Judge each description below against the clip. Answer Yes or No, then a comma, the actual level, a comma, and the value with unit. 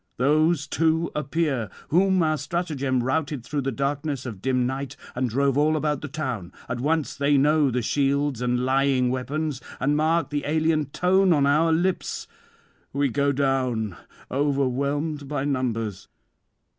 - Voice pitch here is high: No, medium, 140 Hz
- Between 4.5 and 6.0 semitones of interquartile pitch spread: No, average, 3.0 semitones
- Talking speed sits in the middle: Yes, average, 150 wpm